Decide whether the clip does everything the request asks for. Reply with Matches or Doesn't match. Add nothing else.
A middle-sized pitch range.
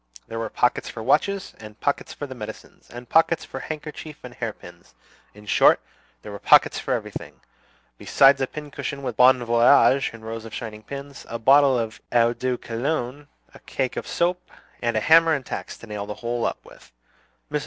Matches